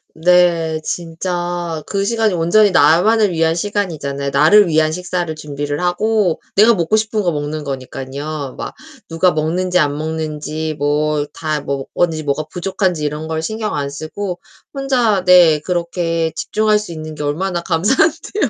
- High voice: No, medium, 165 Hz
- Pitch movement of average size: Yes, average, 3.6 semitones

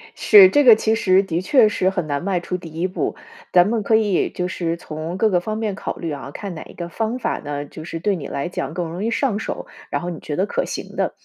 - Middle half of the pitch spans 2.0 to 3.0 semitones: No, average, 4.4 semitones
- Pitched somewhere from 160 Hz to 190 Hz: Yes, medium, 185 Hz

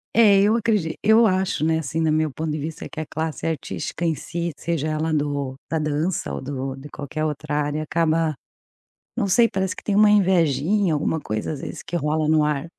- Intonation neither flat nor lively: Yes, average, 3.5 semitones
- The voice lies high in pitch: No, medium, 160 Hz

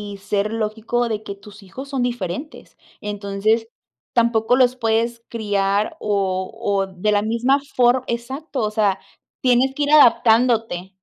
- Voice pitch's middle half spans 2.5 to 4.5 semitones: Yes, average, 3.2 semitones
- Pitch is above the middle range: Yes, high, 225 Hz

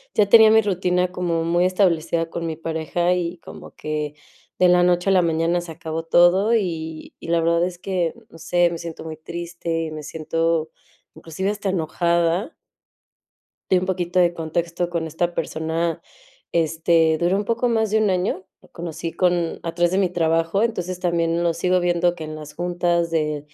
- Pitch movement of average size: No, narrow, 1.7 semitones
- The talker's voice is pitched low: No, medium, 170 Hz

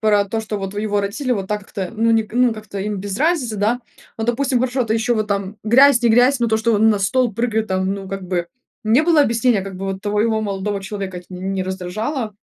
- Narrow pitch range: No, average, 3.2 semitones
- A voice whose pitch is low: No, high, 215 Hz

